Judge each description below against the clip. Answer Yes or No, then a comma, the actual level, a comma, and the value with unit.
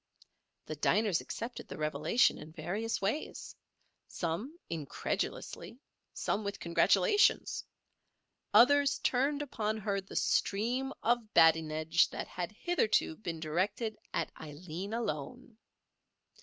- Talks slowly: Yes, slow, 100 wpm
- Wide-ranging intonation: Yes, wide, 6.6 semitones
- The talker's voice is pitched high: Yes, high, 205 Hz